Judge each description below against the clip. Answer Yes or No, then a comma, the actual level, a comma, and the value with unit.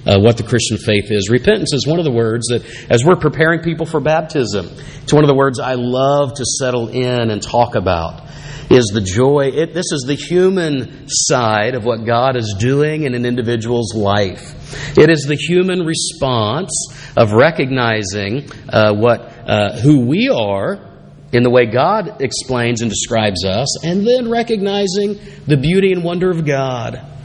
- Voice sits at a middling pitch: No, low, 130 Hz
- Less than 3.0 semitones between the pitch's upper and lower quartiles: No, average, 4.6 semitones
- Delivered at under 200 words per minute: Yes, average, 175 wpm